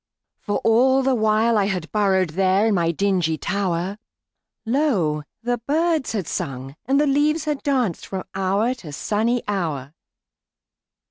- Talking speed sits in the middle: No, slow, 130 wpm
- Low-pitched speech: No, high, 210 Hz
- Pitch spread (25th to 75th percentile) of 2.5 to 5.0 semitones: No, wide, 5.6 semitones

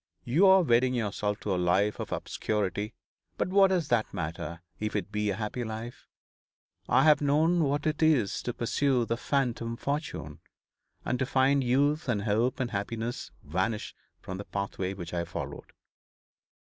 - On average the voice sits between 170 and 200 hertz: No, low, 120 Hz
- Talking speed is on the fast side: No, average, 165 wpm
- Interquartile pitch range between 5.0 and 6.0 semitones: Yes, average, 5.3 semitones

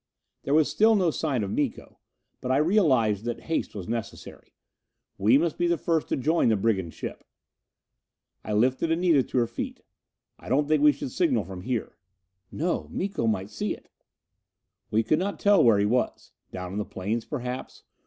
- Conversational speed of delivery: Yes, average, 185 wpm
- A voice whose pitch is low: Yes, low, 130 Hz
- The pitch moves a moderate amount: No, wide, 6.8 semitones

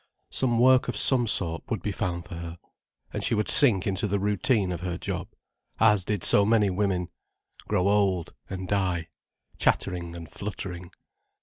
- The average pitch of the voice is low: Yes, very low, 95 Hz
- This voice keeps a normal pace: Yes, average, 175 wpm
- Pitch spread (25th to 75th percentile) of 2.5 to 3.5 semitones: Yes, average, 3.1 semitones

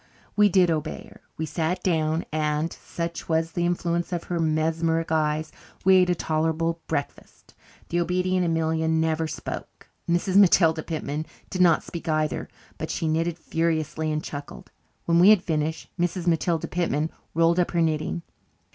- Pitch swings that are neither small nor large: No, narrow, 1.6 semitones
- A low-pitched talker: No, medium, 165 Hz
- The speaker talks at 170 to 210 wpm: No, average, 160 wpm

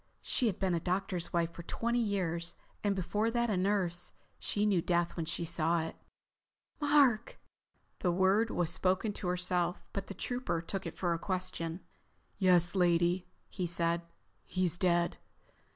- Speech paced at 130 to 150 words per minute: No, average, 160 wpm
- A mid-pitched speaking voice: Yes, medium, 180 Hz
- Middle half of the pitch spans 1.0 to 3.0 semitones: Yes, average, 2.7 semitones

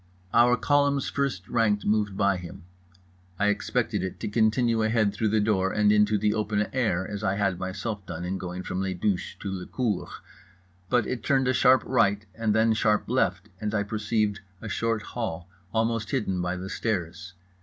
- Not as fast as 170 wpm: No, average, 185 wpm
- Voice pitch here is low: Yes, low, 105 Hz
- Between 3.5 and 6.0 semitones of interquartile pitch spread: No, average, 3.0 semitones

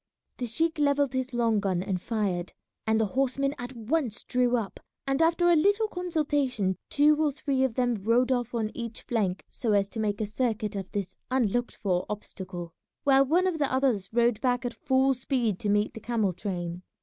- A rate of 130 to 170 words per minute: No, average, 195 wpm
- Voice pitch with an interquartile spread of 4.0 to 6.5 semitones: Yes, average, 4.6 semitones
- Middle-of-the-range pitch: No, high, 240 Hz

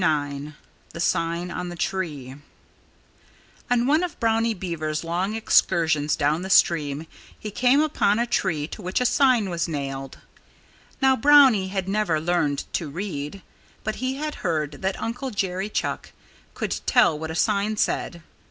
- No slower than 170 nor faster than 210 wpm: No, average, 155 wpm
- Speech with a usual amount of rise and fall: No, wide, 6.0 semitones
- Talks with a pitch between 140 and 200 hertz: Yes, medium, 185 Hz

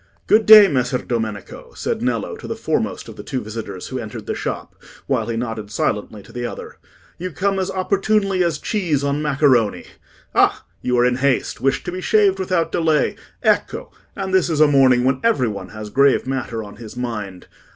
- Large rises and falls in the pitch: Yes, wide, 7.8 semitones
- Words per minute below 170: No, average, 190 wpm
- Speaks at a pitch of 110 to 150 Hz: Yes, low, 135 Hz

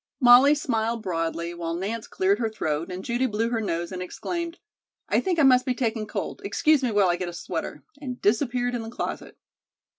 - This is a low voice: No, high, 225 Hz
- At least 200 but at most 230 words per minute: Yes, fast, 205 wpm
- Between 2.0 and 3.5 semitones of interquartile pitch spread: No, wide, 5.5 semitones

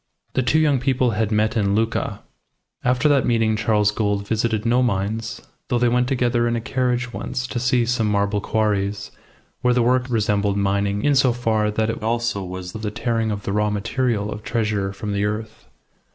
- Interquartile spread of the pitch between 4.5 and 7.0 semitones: No, average, 2.9 semitones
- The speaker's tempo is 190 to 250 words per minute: Yes, average, 195 wpm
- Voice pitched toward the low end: Yes, low, 110 Hz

